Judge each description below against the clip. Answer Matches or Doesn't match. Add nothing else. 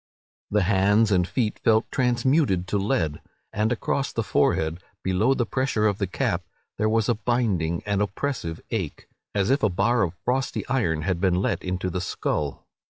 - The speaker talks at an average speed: Matches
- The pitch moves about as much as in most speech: Matches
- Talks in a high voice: Doesn't match